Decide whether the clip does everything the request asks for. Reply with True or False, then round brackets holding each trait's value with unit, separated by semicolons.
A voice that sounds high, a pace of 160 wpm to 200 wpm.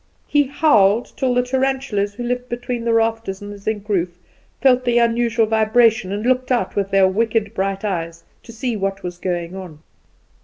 True (220 Hz; 185 wpm)